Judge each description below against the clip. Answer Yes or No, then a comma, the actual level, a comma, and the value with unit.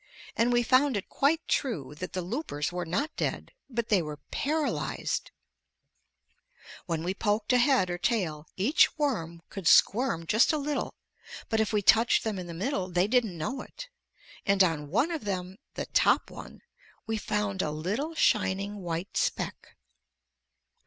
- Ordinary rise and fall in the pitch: No, wide, 6.0 semitones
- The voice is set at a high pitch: Yes, high, 205 Hz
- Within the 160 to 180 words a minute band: Yes, average, 165 wpm